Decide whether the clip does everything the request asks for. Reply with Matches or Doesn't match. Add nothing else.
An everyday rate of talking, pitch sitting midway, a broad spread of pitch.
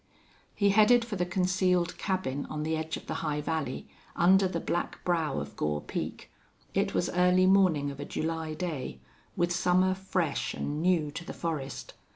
Doesn't match